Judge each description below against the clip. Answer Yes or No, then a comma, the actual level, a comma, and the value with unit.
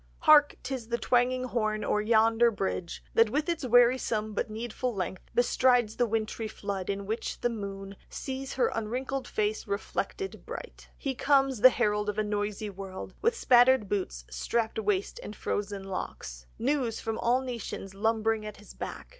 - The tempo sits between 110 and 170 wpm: Yes, average, 165 wpm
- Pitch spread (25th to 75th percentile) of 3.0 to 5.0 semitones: Yes, average, 3.3 semitones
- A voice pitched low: No, high, 225 Hz